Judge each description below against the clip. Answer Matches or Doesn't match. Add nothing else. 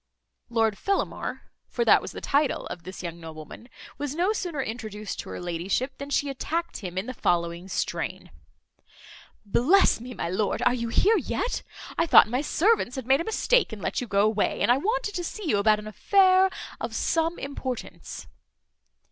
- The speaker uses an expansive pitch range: Matches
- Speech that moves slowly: Doesn't match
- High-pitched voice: Matches